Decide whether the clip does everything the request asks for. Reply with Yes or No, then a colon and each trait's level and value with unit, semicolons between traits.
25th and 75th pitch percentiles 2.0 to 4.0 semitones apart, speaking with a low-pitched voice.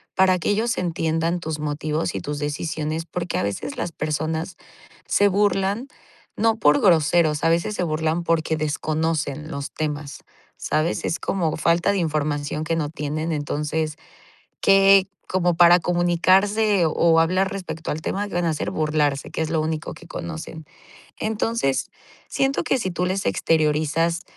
No: average, 2.9 semitones; medium, 165 Hz